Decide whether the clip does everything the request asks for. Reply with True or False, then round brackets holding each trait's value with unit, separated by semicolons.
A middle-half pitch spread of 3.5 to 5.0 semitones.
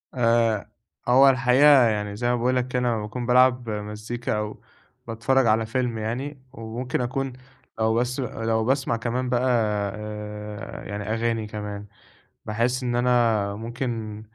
False (2.7 semitones)